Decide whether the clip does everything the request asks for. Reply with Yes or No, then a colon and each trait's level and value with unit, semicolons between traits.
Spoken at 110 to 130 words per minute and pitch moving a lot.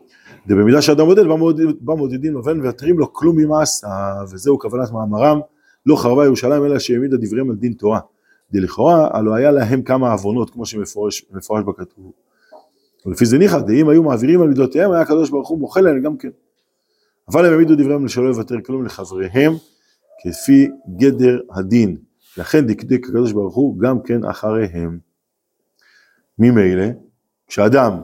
No: fast, 150 wpm; wide, 5.7 semitones